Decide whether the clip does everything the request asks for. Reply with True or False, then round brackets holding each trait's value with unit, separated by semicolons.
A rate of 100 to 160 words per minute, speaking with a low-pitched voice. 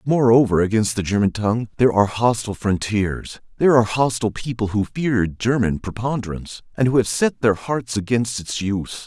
False (170 wpm; 110 Hz)